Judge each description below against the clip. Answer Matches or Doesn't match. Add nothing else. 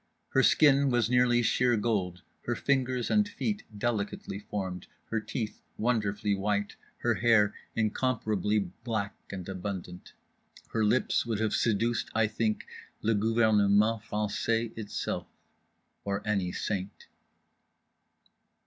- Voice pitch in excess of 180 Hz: Doesn't match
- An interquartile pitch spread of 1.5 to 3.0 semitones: Matches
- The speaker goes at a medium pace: Doesn't match